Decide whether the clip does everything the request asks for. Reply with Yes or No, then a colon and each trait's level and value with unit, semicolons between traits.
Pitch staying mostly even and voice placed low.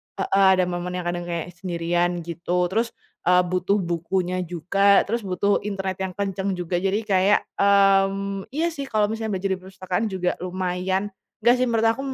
No: narrow, 1.9 semitones; high, 190 Hz